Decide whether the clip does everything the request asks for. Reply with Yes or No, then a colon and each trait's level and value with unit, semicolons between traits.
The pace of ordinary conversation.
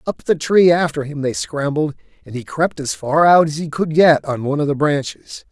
No: fast, 240 wpm